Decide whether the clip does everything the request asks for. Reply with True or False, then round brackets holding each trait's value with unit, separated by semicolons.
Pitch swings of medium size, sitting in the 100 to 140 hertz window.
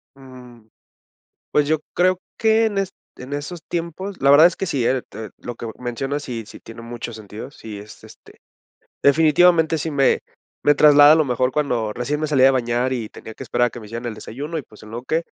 True (4.8 semitones; 135 Hz)